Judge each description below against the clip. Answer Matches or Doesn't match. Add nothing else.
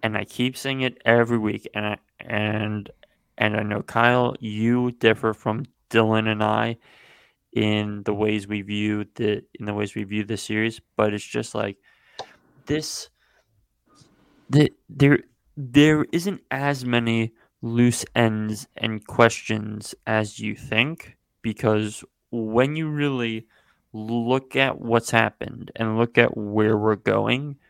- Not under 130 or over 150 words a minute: Matches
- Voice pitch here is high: Doesn't match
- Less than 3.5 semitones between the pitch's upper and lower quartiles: Matches